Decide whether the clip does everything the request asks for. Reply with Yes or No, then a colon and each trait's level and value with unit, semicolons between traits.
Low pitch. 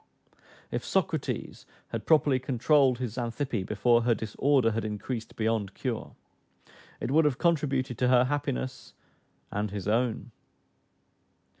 Yes: low, 125 Hz